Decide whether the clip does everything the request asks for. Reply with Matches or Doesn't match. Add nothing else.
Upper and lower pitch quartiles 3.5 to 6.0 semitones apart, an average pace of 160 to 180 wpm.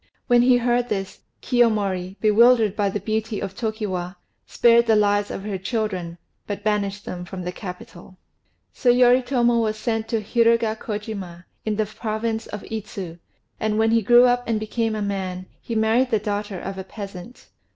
Doesn't match